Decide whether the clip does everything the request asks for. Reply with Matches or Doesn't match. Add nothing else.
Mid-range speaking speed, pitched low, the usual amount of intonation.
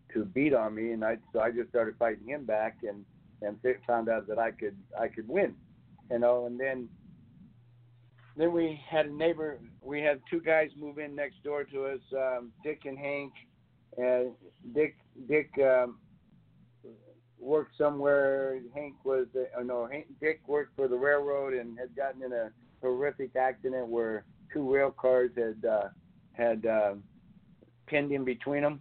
Matches